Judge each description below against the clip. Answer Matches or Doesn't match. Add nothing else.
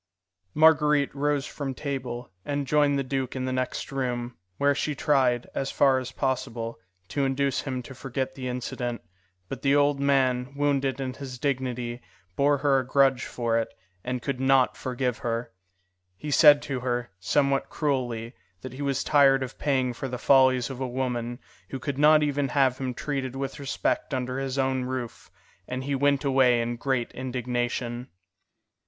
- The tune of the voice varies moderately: Doesn't match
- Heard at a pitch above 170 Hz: Doesn't match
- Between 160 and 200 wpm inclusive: Matches